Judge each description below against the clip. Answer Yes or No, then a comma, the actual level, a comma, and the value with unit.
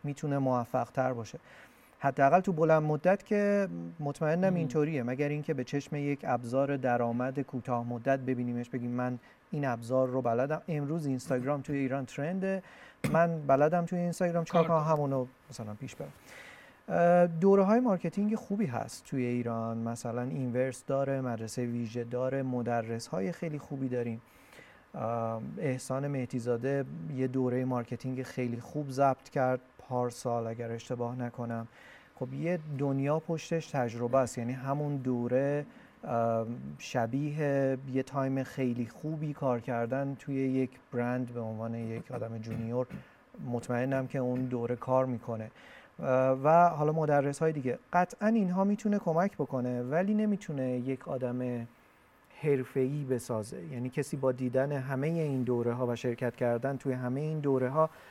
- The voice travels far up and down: No, average, 3.5 semitones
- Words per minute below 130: No, average, 140 wpm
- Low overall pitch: Yes, low, 130 Hz